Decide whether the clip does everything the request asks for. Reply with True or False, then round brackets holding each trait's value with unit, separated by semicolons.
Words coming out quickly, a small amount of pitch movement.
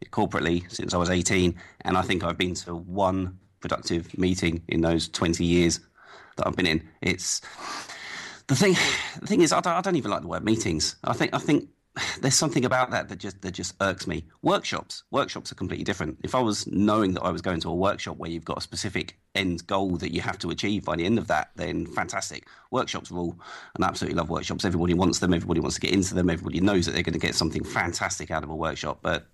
True (240 wpm; 2.3 semitones)